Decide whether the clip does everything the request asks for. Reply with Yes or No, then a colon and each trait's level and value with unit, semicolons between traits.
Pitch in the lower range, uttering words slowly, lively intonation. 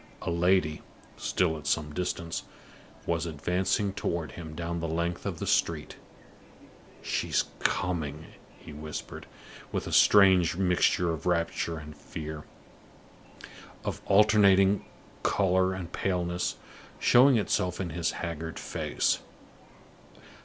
No: very low, 85 Hz; slow, 115 wpm; narrow, 2.6 semitones